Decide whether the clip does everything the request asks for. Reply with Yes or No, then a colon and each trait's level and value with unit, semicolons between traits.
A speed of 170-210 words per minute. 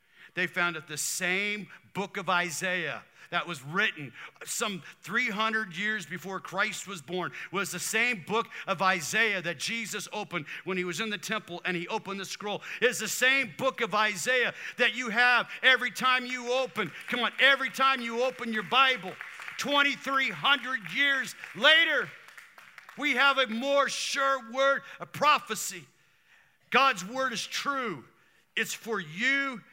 No: average, 155 wpm